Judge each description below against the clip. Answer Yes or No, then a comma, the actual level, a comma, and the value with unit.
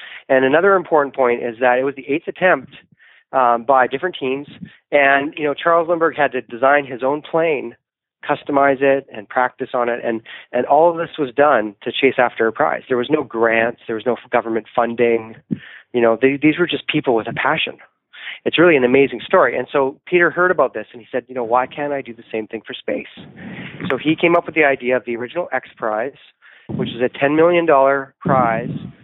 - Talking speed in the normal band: No, fast, 220 wpm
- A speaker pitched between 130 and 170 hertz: Yes, low, 135 Hz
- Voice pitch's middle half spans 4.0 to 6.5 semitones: No, average, 3.6 semitones